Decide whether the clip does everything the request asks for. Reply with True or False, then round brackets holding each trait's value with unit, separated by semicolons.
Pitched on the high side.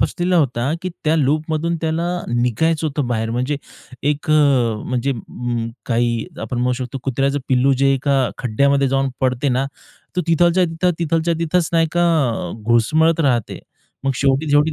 False (140 Hz)